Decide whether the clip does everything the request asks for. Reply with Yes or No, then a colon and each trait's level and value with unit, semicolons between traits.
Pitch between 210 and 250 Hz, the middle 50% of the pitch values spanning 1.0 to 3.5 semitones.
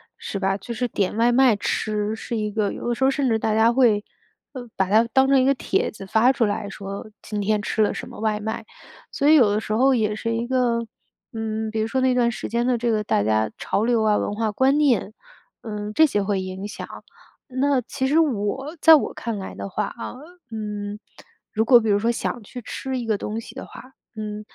Yes: high, 220 Hz; average, 3.1 semitones